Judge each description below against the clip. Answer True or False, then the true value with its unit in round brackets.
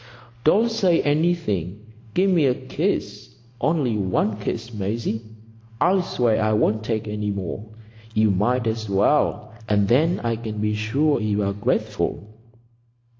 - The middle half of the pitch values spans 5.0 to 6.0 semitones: True (5.6 semitones)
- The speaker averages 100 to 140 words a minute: True (135 wpm)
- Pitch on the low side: True (110 Hz)